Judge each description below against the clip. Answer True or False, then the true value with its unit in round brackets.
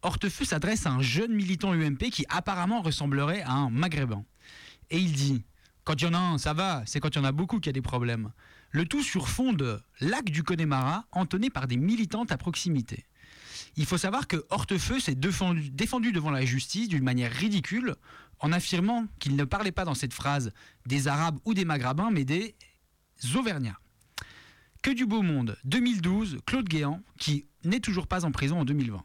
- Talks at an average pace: True (200 wpm)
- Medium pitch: True (160 Hz)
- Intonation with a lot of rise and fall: True (5.7 semitones)